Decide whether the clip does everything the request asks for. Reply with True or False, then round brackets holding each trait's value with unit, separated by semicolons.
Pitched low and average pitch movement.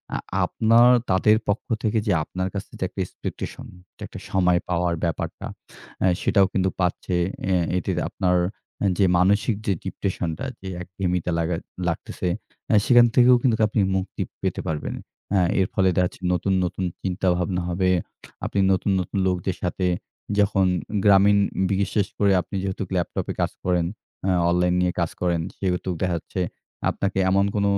False (95 Hz; 1.9 semitones)